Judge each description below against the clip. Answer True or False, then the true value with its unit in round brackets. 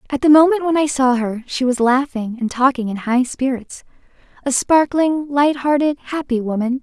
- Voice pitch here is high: True (265 Hz)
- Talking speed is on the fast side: False (165 wpm)